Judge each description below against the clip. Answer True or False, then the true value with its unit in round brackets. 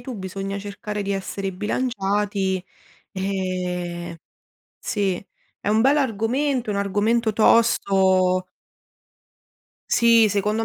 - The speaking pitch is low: False (200 Hz)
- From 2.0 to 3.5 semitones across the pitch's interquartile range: True (2.9 semitones)